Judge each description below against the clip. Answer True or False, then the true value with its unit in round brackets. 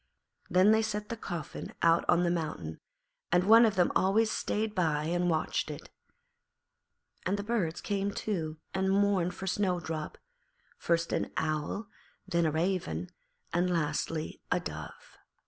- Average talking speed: True (145 wpm)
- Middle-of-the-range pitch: True (180 Hz)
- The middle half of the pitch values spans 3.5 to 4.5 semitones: True (3.8 semitones)